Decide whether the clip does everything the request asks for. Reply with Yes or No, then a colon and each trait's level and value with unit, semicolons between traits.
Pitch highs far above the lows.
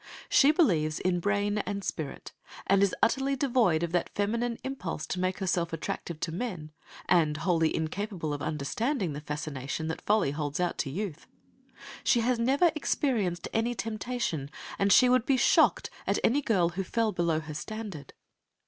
Yes: wide, 6.4 semitones